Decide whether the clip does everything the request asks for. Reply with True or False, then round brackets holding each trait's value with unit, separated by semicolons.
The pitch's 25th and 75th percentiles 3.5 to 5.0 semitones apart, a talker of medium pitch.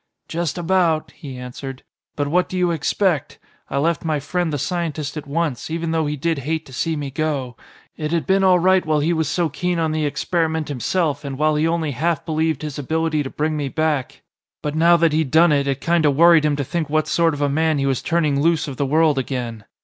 False (2.7 semitones; 155 Hz)